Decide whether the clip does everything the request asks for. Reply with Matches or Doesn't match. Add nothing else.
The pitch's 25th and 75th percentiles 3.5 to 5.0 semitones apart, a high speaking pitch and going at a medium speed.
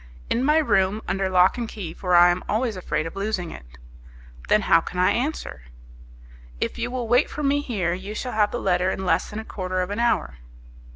Doesn't match